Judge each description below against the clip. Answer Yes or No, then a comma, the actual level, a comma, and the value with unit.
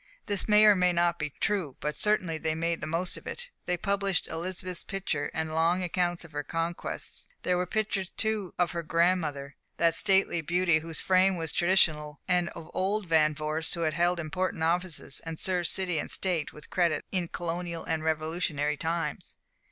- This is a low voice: No, medium, 170 Hz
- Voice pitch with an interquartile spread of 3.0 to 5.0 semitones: No, narrow, 2.5 semitones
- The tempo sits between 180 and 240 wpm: Yes, average, 185 wpm